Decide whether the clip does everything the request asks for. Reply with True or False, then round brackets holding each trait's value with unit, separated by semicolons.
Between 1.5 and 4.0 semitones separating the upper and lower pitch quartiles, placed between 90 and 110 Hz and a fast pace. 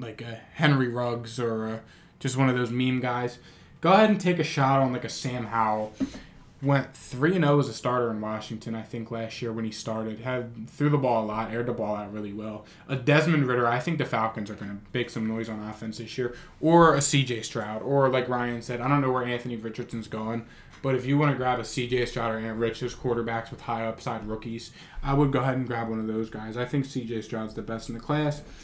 False (3.2 semitones; 120 Hz; 245 wpm)